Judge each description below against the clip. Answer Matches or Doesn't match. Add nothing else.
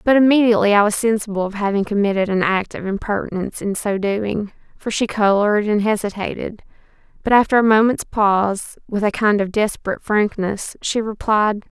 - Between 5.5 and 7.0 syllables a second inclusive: Matches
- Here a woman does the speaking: Matches